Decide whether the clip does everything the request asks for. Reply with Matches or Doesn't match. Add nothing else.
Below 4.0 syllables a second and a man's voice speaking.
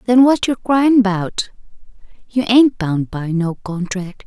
Doesn't match